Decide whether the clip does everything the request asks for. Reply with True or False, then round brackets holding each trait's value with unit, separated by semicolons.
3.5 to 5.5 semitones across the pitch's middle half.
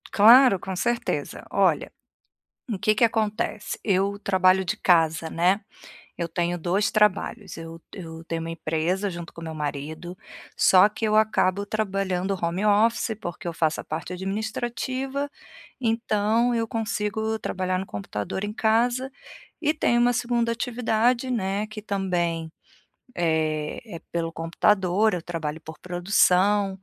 True (4.4 semitones)